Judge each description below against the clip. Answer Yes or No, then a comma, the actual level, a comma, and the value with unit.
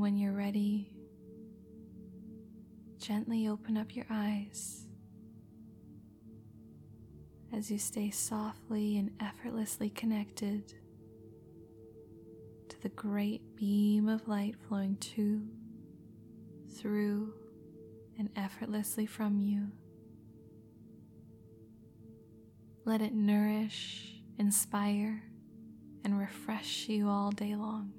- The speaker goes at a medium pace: No, slow, 80 wpm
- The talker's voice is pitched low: No, high, 205 Hz